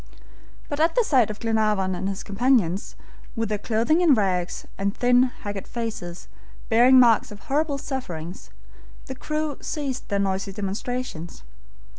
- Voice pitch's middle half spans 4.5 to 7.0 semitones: Yes, average, 5.0 semitones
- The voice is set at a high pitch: Yes, high, 225 Hz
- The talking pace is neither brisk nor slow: Yes, average, 145 wpm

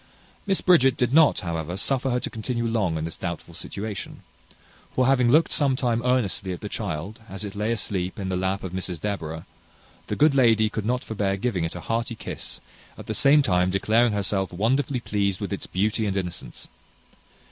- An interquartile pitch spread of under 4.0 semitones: No, average, 4.7 semitones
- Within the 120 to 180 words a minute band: No, average, 195 wpm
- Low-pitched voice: Yes, low, 105 Hz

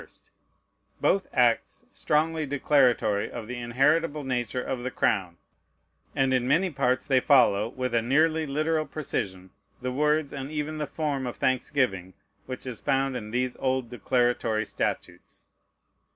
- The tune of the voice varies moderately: Yes, average, 3.4 semitones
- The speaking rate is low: No, average, 145 wpm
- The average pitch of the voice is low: Yes, low, 130 Hz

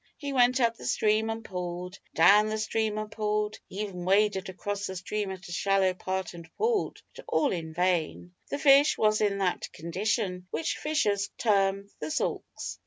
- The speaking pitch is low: No, high, 200 Hz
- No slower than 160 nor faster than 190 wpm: Yes, average, 180 wpm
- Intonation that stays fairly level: No, average, 3.0 semitones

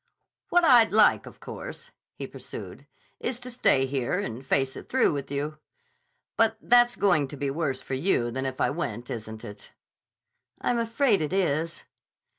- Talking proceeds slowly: No, average, 170 wpm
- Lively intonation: Yes, wide, 9.0 semitones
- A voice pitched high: No, medium, 155 Hz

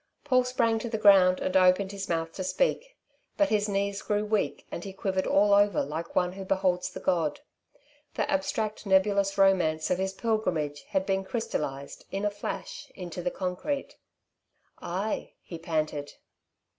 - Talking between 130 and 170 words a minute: Yes, average, 165 wpm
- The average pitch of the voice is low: No, high, 195 Hz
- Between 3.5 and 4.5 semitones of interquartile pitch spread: No, average, 2.8 semitones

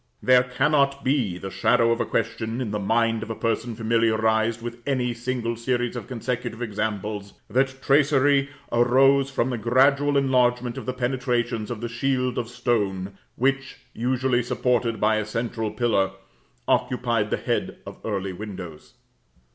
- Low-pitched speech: Yes, low, 120 Hz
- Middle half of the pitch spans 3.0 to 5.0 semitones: No, narrow, 2.4 semitones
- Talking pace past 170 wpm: No, average, 155 wpm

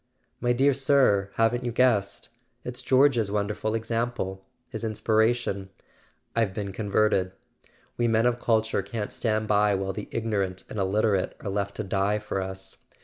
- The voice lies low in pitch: Yes, low, 110 Hz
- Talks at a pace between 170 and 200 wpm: No, average, 150 wpm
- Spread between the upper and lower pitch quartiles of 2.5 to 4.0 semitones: Yes, average, 2.9 semitones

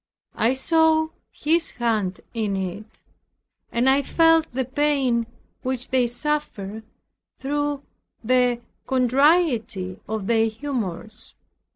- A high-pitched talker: Yes, very high, 250 Hz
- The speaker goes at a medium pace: No, slow, 100 wpm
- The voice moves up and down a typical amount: Yes, average, 4.9 semitones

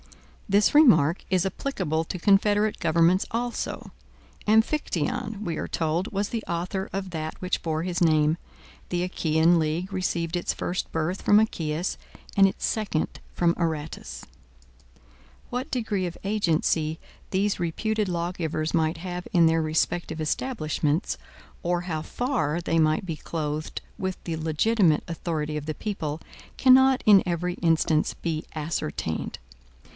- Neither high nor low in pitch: Yes, medium, 170 Hz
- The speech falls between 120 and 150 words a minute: Yes, slow, 135 wpm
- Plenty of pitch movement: No, average, 3.7 semitones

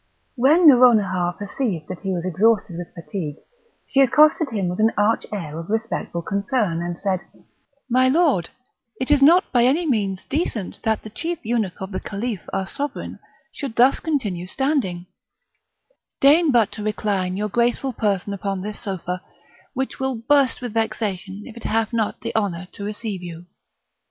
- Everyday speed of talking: Yes, average, 165 wpm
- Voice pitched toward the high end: Yes, high, 215 Hz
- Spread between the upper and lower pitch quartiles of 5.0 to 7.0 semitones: Yes, wide, 5.4 semitones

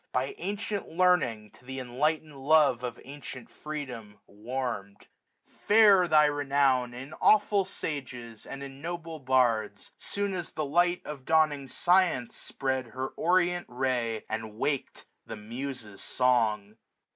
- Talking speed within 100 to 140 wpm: Yes, slow, 135 wpm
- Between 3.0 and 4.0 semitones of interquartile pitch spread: No, average, 4.7 semitones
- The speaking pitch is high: No, low, 135 Hz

